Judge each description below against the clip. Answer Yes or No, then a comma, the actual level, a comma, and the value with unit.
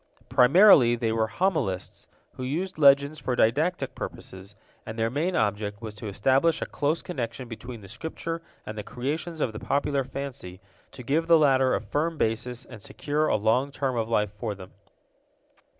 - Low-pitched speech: Yes, low, 125 Hz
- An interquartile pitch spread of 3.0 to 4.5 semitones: No, average, 5.2 semitones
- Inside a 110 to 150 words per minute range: No, average, 175 wpm